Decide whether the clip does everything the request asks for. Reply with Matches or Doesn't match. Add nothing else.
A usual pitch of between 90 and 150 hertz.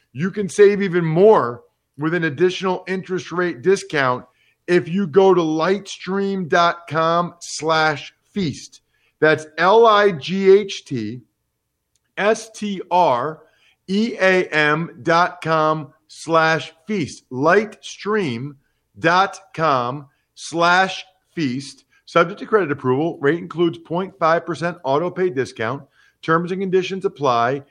Doesn't match